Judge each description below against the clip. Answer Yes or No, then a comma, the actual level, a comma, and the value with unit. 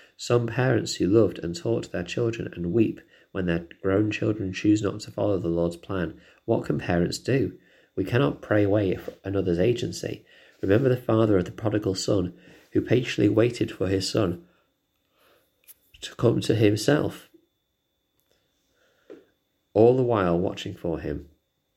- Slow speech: No, average, 150 wpm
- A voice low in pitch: Yes, low, 105 Hz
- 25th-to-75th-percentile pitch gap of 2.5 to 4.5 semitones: Yes, average, 3.8 semitones